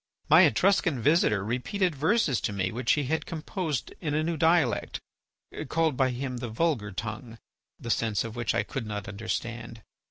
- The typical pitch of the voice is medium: No, low, 125 Hz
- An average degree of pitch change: No, wide, 6.3 semitones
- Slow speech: No, average, 170 wpm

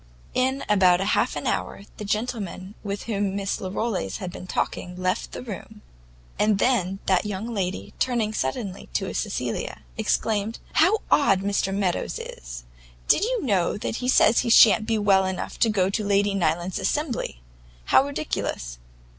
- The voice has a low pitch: No, high, 200 Hz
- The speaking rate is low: No, average, 155 wpm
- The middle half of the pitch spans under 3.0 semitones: No, average, 3.3 semitones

